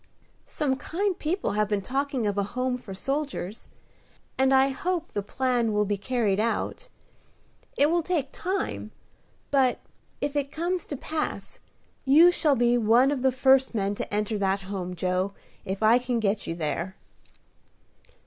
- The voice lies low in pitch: No, very high, 250 Hz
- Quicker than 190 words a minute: No, average, 160 wpm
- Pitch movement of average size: No, wide, 5.8 semitones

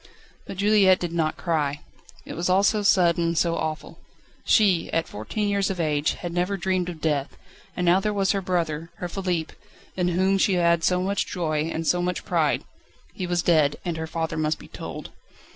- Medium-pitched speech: Yes, medium, 175 Hz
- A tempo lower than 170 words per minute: No, average, 195 wpm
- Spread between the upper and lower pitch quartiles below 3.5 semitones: Yes, average, 2.7 semitones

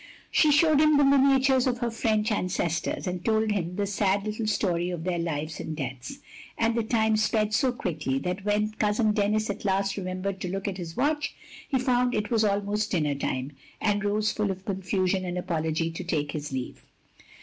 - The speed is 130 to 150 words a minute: No, fast, 205 wpm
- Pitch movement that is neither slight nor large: Yes, average, 3.7 semitones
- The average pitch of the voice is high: Yes, high, 205 Hz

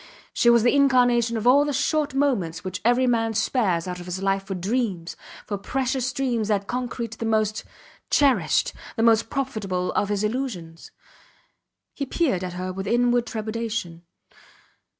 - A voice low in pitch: No, high, 225 Hz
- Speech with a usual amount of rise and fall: Yes, average, 4.5 semitones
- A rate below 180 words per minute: Yes, average, 160 wpm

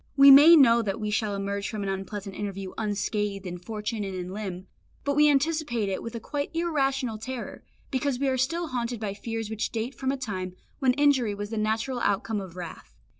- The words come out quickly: Yes, fast, 210 wpm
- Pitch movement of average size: Yes, average, 4.9 semitones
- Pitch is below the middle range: No, high, 225 Hz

